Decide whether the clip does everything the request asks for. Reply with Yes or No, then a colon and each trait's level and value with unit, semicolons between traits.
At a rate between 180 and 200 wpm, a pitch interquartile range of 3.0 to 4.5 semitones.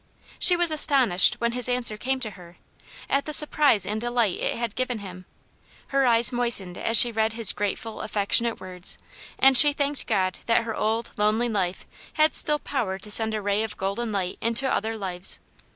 Yes: average, 190 wpm; average, 3.7 semitones